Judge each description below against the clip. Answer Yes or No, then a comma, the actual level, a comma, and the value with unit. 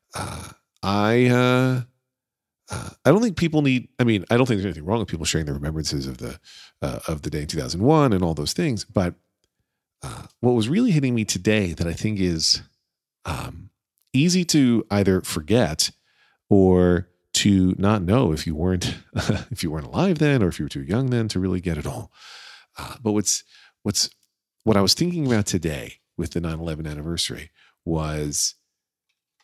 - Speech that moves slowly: No, average, 185 wpm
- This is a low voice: Yes, low, 100 Hz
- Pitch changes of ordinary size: No, wide, 6.5 semitones